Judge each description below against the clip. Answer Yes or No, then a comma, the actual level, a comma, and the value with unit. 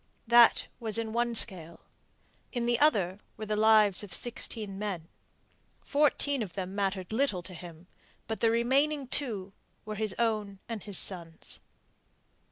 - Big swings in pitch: No, average, 3.6 semitones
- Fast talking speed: No, average, 150 wpm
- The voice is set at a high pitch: Yes, high, 215 Hz